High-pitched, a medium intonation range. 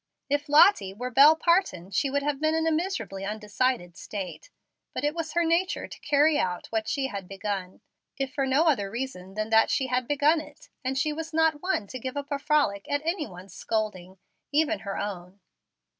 No: very high, 265 Hz; wide, 7.2 semitones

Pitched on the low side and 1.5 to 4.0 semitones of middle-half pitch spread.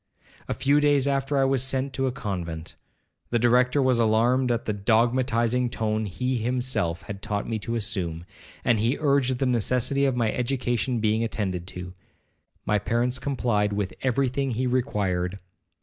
Yes: low, 120 Hz; average, 3.7 semitones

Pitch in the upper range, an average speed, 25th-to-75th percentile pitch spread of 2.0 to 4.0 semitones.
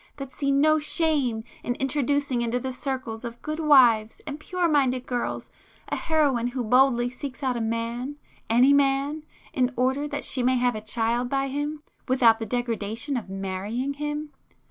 Yes: very high, 255 Hz; average, 170 wpm; average, 3.2 semitones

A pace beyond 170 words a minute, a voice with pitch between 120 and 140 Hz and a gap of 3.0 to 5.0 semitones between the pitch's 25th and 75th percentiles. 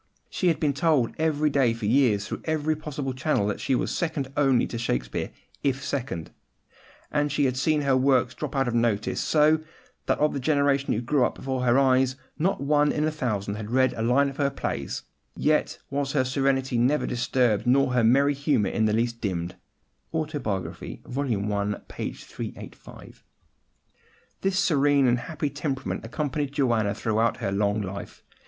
Yes: average, 180 wpm; low, 135 Hz; average, 3.8 semitones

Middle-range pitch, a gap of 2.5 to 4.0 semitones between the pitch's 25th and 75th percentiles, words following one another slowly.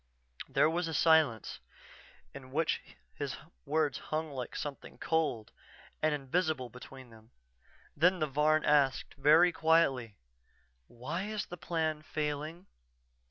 Yes: medium, 155 Hz; average, 3.3 semitones; slow, 120 wpm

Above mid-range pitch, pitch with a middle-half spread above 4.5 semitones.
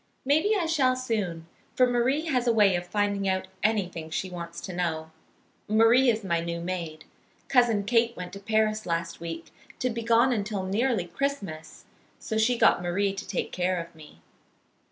Yes: high, 200 Hz; wide, 5.4 semitones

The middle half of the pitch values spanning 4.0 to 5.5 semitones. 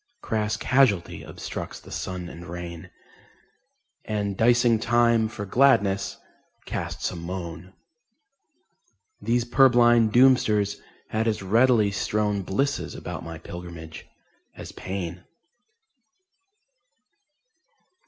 Yes: average, 4.7 semitones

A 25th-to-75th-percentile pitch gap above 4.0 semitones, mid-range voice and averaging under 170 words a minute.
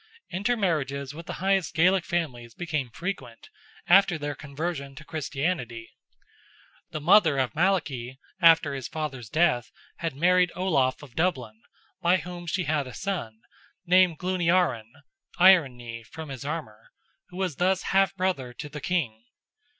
Yes: wide, 5.4 semitones; medium, 155 Hz; average, 145 wpm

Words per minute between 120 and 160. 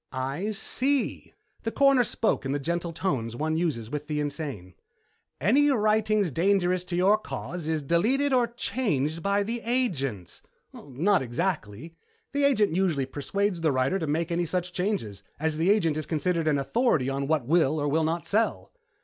No: average, 170 wpm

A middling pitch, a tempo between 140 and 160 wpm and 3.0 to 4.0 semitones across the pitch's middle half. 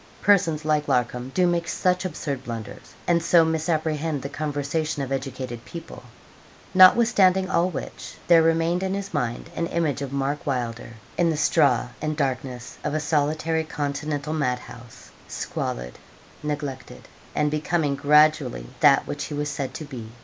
Yes: medium, 150 Hz; average, 155 wpm; average, 3.3 semitones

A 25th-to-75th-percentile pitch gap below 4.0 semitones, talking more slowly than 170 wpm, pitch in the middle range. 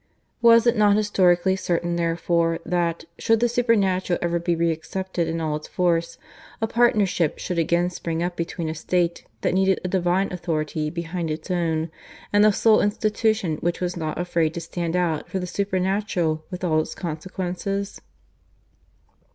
Yes: narrow, 2.6 semitones; average, 160 wpm; medium, 175 Hz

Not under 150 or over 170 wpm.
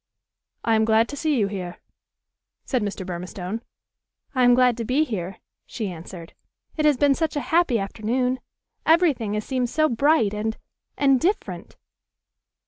Yes: average, 160 wpm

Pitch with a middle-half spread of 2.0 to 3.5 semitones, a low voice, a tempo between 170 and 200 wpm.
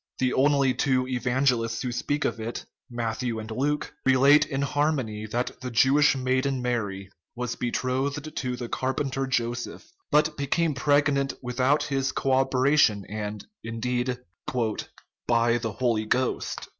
No: average, 2.8 semitones; low, 130 Hz; average, 140 wpm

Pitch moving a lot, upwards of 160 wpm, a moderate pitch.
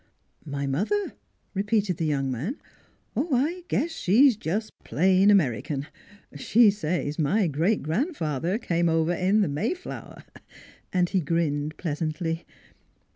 No: wide, 5.7 semitones; average, 140 wpm; medium, 175 Hz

